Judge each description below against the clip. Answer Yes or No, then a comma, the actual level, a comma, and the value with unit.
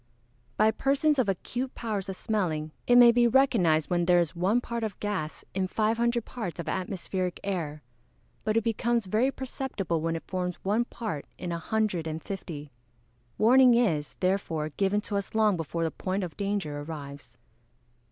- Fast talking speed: No, average, 180 wpm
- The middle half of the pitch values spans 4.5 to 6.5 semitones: Yes, average, 5.3 semitones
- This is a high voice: Yes, high, 195 Hz